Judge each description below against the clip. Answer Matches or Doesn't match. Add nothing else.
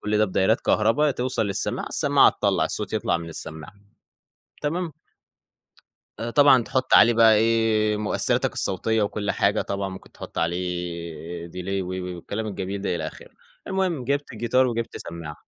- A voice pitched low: Matches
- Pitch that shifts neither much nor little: Matches